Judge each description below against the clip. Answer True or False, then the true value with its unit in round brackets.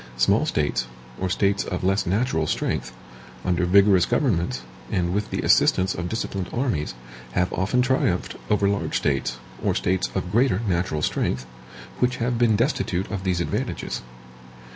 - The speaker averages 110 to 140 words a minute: False (150 wpm)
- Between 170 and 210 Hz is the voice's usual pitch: False (95 Hz)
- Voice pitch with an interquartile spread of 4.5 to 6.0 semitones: False (3.4 semitones)